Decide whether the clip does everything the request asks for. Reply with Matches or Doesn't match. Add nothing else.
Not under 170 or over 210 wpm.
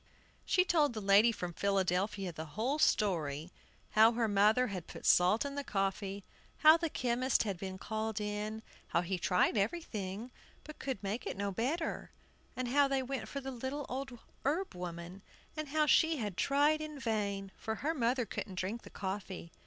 Matches